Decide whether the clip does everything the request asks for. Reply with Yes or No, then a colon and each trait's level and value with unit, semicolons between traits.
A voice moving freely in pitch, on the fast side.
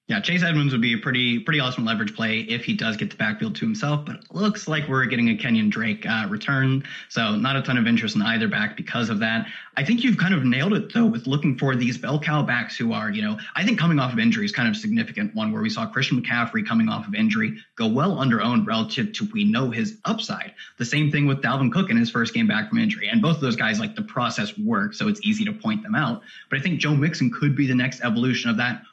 Yes: wide, 8.2 semitones; fast, 275 wpm